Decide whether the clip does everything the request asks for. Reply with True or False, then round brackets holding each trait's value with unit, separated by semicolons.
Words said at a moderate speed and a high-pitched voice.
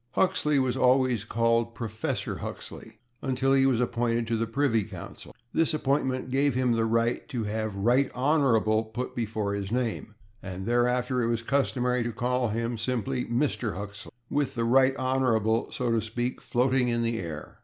False (170 wpm; 120 Hz)